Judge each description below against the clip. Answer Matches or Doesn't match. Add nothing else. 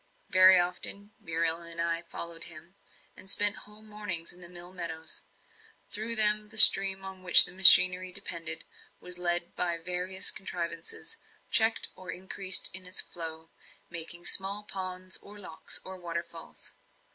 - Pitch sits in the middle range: Matches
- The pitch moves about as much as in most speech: Doesn't match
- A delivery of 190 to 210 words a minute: Doesn't match